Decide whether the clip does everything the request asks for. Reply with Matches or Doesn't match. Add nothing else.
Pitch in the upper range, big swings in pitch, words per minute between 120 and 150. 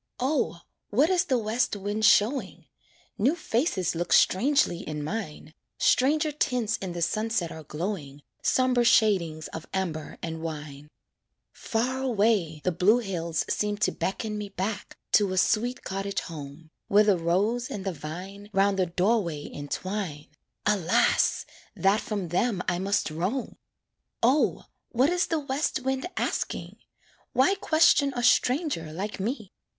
Matches